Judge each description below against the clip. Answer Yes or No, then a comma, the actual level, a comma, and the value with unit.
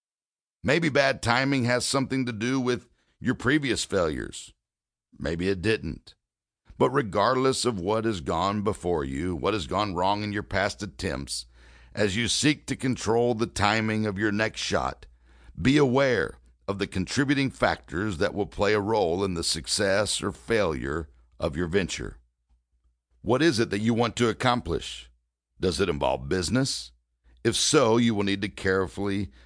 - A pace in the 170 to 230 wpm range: No, average, 160 wpm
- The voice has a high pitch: No, low, 100 Hz